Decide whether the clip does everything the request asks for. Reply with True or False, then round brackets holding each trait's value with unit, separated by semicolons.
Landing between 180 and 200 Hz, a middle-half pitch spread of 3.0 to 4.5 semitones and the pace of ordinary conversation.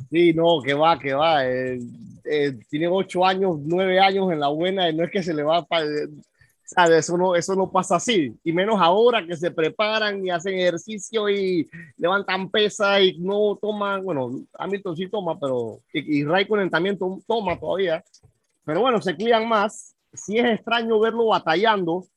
True (185 Hz; 3.8 semitones; 185 wpm)